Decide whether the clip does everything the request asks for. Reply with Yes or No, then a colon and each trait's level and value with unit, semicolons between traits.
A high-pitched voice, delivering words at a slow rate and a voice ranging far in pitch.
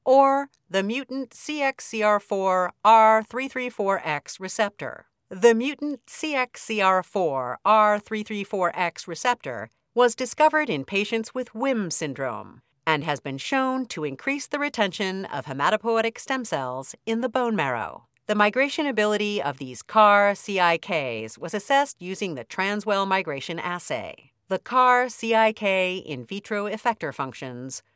Yes: high, 210 Hz; slow, 115 wpm; wide, 5.7 semitones